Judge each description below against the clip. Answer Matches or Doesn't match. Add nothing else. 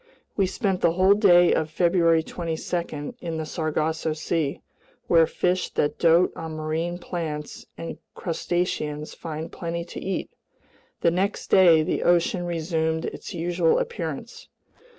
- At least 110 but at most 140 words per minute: Matches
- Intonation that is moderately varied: Doesn't match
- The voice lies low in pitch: Doesn't match